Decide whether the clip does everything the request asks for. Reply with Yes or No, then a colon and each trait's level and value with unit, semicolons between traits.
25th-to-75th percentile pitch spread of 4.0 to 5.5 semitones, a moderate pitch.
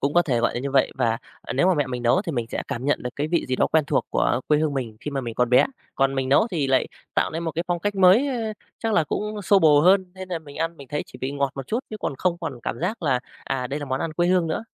Yes: average, 5.1 semitones; medium, 150 Hz